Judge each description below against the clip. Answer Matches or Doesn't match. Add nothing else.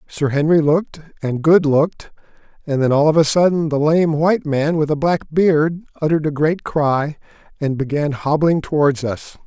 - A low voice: Doesn't match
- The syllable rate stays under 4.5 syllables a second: Doesn't match